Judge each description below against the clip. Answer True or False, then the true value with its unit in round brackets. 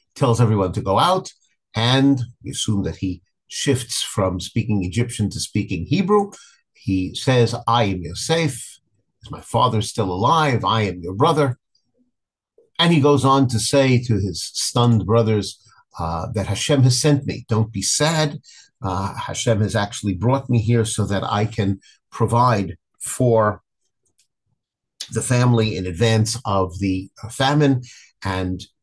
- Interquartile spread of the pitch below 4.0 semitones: False (4.9 semitones)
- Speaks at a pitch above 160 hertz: False (115 Hz)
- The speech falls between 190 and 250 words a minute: False (150 wpm)